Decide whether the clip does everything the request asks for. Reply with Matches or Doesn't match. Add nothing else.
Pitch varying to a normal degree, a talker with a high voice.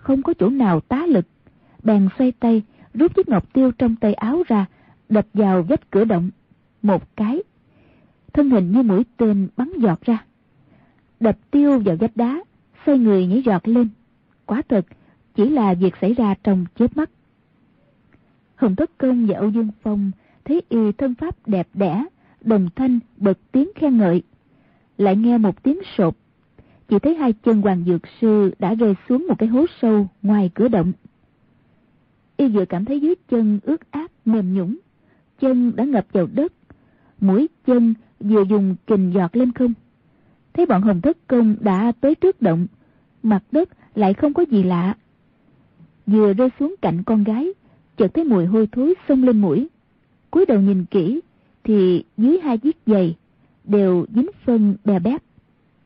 Matches